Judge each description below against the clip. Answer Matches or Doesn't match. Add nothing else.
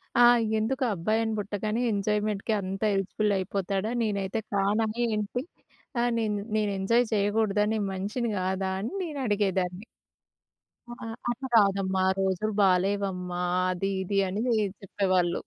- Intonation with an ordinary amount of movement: Doesn't match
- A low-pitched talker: Doesn't match